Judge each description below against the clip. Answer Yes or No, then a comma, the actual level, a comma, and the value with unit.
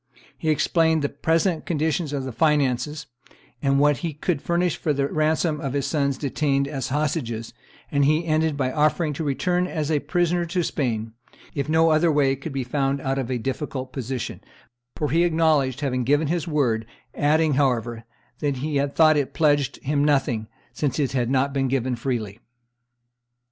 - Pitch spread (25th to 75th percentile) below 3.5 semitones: Yes, average, 2.8 semitones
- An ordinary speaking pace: Yes, average, 180 wpm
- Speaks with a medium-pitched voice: Yes, medium, 145 Hz